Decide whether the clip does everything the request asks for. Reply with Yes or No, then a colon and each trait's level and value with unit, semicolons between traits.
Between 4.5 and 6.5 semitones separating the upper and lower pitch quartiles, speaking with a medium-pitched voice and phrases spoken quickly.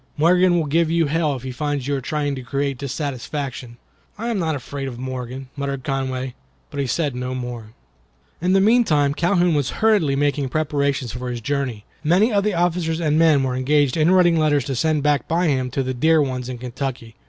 No: average, 3.9 semitones; medium, 145 Hz; fast, 210 wpm